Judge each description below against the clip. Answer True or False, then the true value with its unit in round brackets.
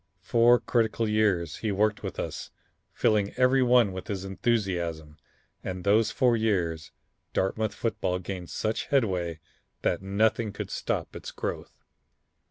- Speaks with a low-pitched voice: True (105 Hz)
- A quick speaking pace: False (135 wpm)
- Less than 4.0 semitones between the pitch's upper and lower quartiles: True (3.6 semitones)